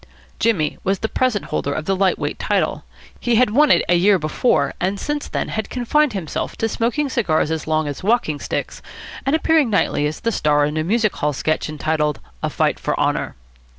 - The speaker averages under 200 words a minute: No, fast, 205 wpm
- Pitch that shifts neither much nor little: No, wide, 7.3 semitones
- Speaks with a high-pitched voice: Yes, high, 195 Hz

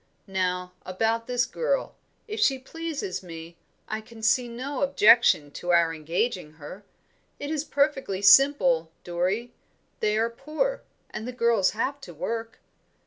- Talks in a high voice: Yes, high, 230 Hz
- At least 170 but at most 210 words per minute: No, average, 140 wpm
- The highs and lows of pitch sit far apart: Yes, wide, 7.0 semitones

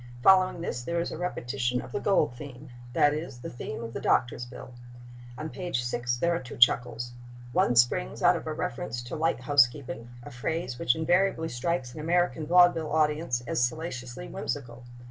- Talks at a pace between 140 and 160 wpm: No, average, 180 wpm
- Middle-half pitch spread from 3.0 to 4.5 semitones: No, average, 4.9 semitones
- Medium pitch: No, low, 130 Hz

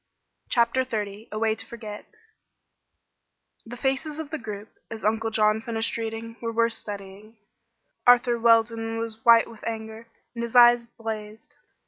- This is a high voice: Yes, high, 225 Hz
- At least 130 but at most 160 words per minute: Yes, average, 145 wpm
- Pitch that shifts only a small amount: Yes, narrow, 1.2 semitones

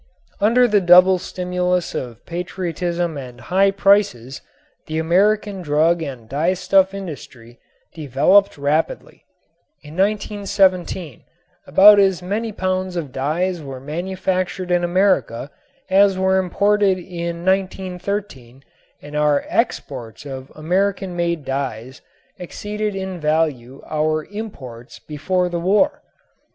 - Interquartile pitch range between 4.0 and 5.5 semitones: Yes, average, 4.4 semitones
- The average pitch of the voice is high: No, medium, 180 Hz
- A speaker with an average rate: No, slow, 110 wpm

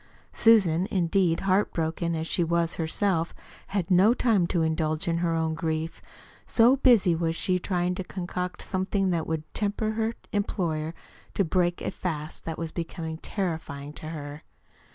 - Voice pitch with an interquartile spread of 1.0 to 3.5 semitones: Yes, average, 3.1 semitones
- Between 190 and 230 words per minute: No, average, 155 wpm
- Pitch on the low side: No, medium, 170 Hz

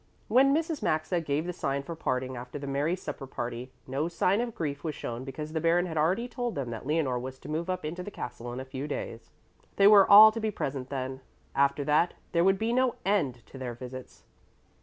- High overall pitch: No, medium, 150 Hz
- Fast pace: Yes, fast, 225 wpm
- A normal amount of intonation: No, wide, 5.9 semitones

